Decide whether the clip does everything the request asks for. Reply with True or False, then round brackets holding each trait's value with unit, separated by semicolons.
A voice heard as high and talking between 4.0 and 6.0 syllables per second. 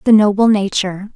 True (205 Hz; 5.8 syllables/s)